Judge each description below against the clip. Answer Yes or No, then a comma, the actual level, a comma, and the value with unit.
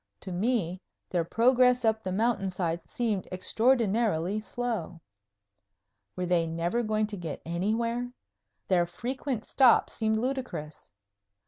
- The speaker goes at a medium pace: No, slow, 120 wpm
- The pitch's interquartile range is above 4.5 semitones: Yes, average, 5.2 semitones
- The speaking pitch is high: Yes, high, 215 Hz